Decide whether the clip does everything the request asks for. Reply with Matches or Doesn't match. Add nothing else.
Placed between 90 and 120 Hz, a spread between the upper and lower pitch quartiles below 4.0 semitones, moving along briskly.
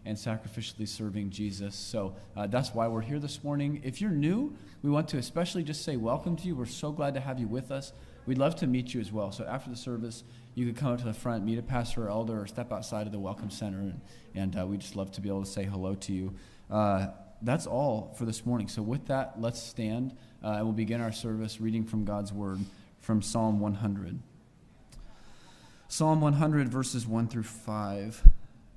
Matches